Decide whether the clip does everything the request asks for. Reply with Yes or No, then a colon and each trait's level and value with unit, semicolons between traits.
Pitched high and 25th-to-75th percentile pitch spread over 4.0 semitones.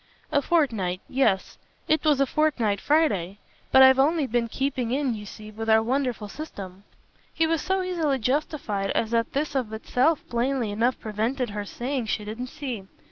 Yes: very high, 250 Hz; average, 4.9 semitones